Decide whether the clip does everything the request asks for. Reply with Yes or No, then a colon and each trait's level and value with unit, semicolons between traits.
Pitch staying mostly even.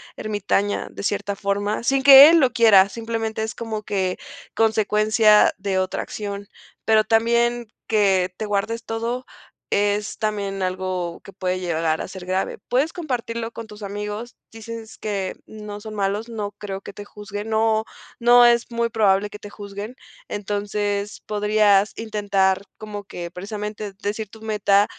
Yes: narrow, 2.0 semitones